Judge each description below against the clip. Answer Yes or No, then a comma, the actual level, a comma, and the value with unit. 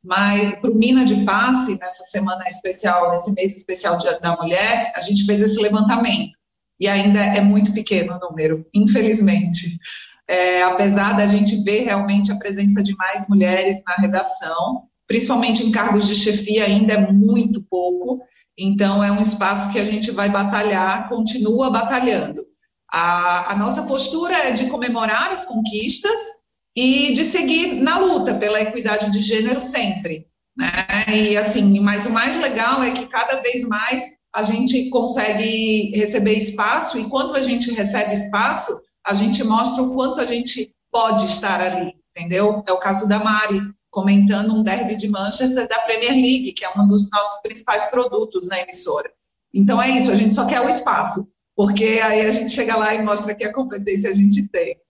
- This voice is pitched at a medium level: No, high, 215 Hz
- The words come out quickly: No, average, 175 wpm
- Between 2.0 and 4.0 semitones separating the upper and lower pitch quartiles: Yes, average, 3.4 semitones